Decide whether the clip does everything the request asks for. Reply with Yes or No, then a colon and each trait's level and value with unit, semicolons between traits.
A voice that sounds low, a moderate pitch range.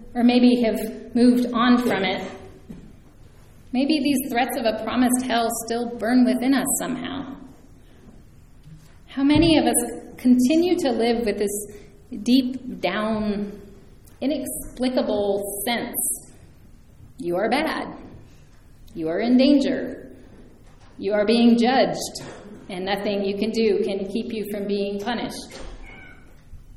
No: high, 235 Hz; average, 3.6 semitones